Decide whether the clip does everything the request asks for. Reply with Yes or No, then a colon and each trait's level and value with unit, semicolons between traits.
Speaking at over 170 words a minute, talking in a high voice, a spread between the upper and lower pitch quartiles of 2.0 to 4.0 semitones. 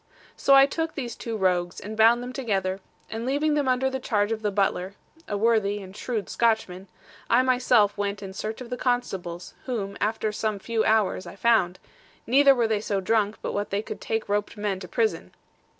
Yes: average, 195 wpm; high, 215 Hz; average, 3.3 semitones